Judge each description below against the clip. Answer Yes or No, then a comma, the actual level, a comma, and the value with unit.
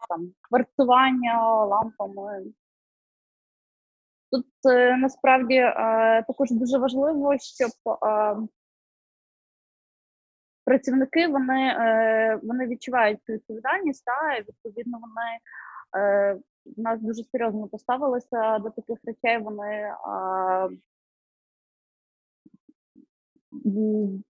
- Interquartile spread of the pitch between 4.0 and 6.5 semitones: No, average, 3.2 semitones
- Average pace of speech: No, slow, 80 wpm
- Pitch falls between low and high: No, high, 230 Hz